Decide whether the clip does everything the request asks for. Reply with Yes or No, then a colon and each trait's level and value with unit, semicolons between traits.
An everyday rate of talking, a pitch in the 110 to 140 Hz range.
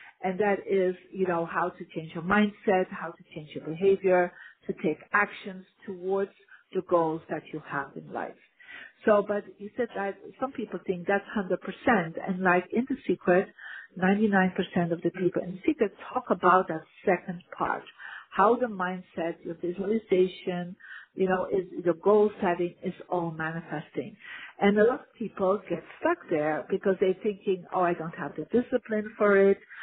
No: average, 175 wpm; high, 190 Hz